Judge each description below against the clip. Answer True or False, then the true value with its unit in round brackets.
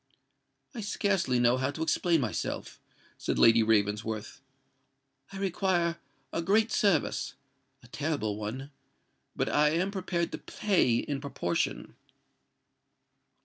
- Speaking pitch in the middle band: True (145 Hz)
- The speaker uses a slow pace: True (110 wpm)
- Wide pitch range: True (7.1 semitones)